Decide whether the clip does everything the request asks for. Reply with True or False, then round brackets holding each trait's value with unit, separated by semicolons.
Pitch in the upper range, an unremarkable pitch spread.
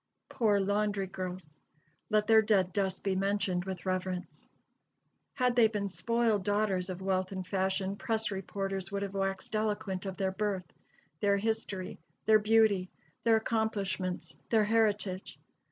False (200 Hz; 2.2 semitones)